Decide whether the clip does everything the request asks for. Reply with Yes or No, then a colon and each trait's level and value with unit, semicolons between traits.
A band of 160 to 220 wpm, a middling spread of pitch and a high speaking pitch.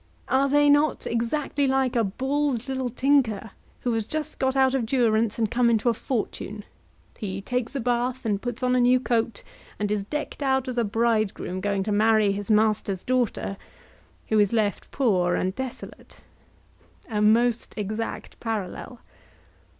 Yes: average, 165 wpm; average, 3.6 semitones; high, 235 Hz